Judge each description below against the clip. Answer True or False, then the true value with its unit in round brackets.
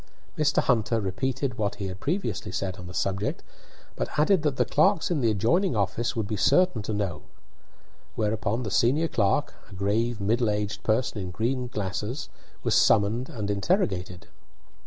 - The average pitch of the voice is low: True (110 Hz)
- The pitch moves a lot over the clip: False (4.6 semitones)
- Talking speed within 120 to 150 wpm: False (165 wpm)